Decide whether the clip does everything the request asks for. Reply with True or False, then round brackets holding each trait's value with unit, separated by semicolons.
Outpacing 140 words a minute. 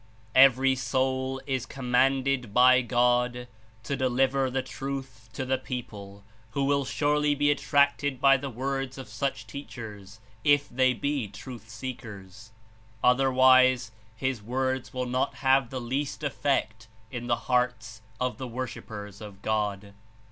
False (135 wpm)